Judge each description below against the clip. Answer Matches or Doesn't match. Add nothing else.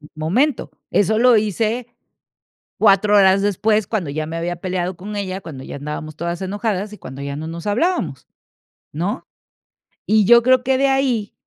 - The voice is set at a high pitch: Matches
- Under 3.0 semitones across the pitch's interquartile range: Doesn't match